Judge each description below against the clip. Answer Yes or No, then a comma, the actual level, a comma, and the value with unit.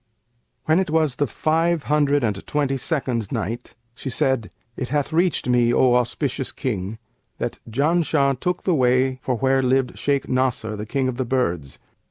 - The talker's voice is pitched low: Yes, low, 130 Hz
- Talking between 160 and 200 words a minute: Yes, average, 170 wpm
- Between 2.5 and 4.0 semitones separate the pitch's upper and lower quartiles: Yes, average, 3.2 semitones